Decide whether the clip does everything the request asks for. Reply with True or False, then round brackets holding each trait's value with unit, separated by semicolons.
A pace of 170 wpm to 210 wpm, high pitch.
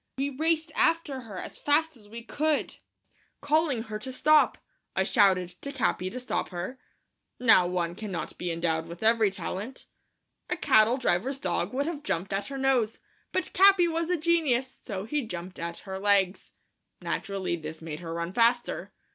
True (175 wpm; 225 Hz)